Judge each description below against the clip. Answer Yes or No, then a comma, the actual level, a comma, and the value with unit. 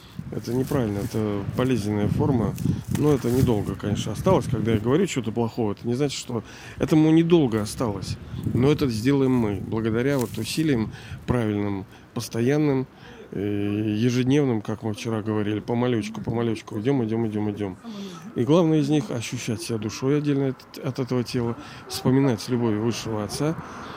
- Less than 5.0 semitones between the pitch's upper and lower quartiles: Yes, average, 3.9 semitones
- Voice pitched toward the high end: No, low, 120 Hz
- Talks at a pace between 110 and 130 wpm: No, average, 150 wpm